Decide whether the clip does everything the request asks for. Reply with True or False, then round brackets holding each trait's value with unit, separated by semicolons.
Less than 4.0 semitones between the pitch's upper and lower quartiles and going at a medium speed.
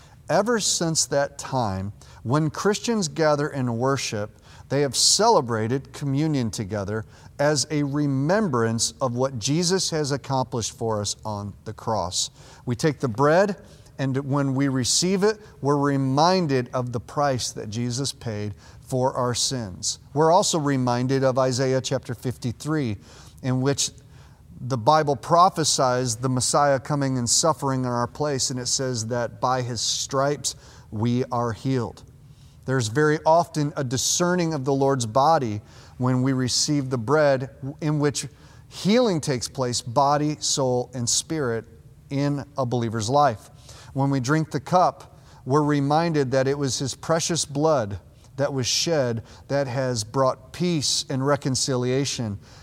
True (3.2 semitones; 145 wpm)